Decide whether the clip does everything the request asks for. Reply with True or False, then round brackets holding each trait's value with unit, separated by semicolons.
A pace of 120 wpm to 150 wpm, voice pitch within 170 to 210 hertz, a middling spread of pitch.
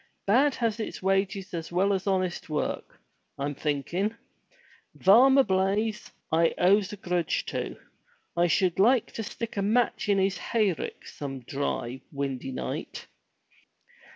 True (145 wpm; 190 Hz; 4.3 semitones)